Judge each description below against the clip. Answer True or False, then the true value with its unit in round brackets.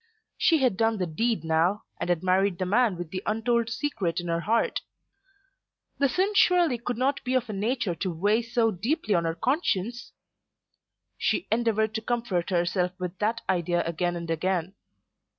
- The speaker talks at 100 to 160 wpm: False (175 wpm)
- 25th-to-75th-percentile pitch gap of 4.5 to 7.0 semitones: True (5.3 semitones)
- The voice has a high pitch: True (210 Hz)